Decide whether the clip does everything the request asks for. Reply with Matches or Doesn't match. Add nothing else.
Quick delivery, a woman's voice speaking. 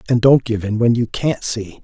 Doesn't match